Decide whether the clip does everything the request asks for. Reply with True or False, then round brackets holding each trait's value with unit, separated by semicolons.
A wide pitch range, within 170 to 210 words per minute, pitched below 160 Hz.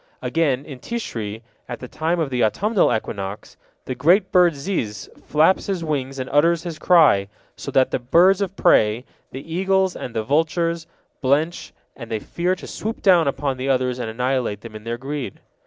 True (5.7 semitones; 185 wpm; 140 Hz)